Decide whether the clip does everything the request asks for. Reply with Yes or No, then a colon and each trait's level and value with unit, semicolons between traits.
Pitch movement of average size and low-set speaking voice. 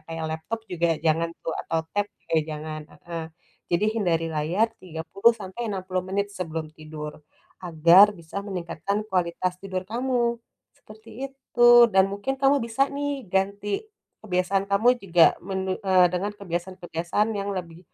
No: average, 3.7 semitones; high, 190 Hz